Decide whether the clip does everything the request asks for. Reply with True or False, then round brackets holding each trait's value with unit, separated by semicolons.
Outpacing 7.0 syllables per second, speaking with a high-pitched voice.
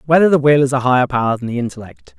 False (7.4 syllables/s; 135 Hz)